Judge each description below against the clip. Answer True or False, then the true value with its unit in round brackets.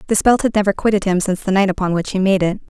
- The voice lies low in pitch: False (195 Hz)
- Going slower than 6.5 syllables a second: False (7.4 syllables/s)